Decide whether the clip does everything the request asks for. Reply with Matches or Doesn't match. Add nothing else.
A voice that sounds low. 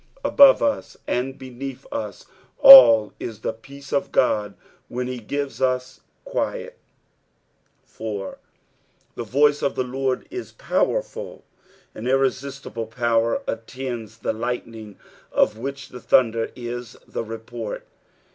Matches